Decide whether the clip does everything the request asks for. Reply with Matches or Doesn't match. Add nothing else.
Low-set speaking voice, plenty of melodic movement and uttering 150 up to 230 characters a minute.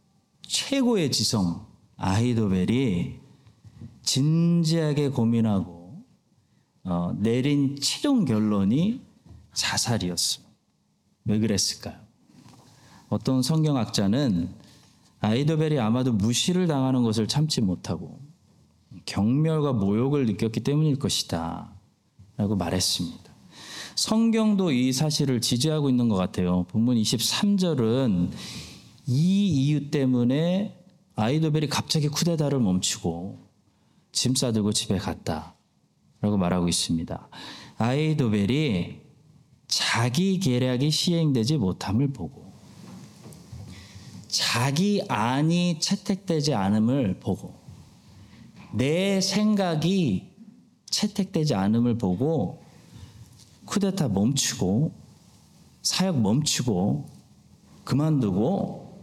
Matches